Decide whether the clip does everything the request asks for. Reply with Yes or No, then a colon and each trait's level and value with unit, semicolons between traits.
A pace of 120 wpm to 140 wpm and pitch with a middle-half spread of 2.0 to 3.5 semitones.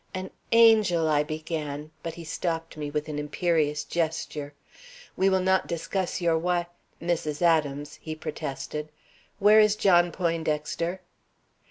Yes: slow, 135 wpm; average, 2.8 semitones